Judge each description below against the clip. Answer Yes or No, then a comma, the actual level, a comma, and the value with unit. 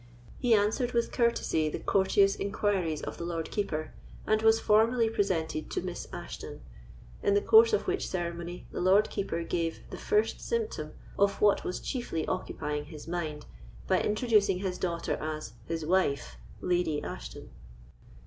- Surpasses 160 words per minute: No, average, 155 wpm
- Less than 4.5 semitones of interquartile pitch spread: No, average, 4.8 semitones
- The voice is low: No, medium, 185 Hz